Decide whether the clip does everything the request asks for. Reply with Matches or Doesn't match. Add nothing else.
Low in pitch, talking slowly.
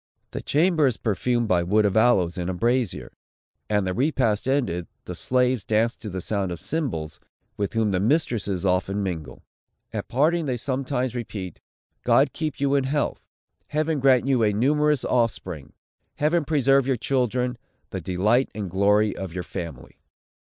Doesn't match